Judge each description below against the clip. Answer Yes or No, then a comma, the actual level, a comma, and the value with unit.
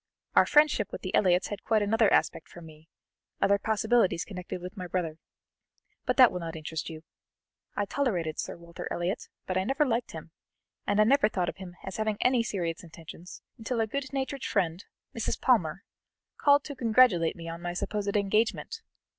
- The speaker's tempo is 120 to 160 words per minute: No, average, 185 wpm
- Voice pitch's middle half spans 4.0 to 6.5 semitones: Yes, average, 5.0 semitones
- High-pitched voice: Yes, high, 200 Hz